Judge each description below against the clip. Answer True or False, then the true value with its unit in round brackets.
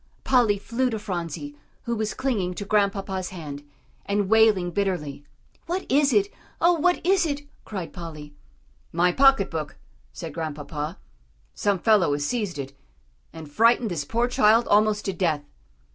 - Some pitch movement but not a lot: False (5.8 semitones)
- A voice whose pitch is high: True (200 Hz)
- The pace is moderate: True (150 wpm)